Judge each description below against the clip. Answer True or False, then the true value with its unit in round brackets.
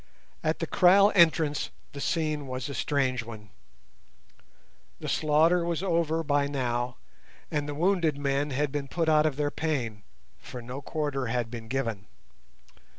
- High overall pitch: False (145 Hz)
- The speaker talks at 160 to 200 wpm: False (150 wpm)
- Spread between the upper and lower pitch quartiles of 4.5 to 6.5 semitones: False (3.8 semitones)